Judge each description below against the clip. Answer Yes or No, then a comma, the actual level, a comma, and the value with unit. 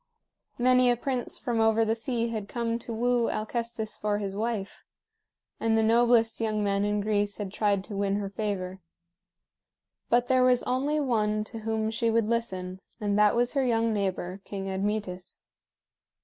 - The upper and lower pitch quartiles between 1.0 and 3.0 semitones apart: Yes, narrow, 2.5 semitones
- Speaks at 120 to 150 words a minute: No, average, 170 wpm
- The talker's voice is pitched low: No, high, 220 Hz